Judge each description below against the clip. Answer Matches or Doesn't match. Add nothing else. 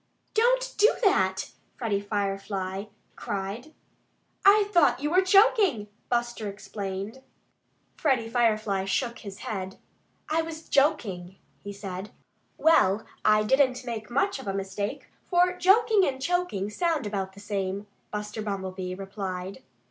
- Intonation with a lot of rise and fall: Matches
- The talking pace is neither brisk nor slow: Doesn't match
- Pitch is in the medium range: Doesn't match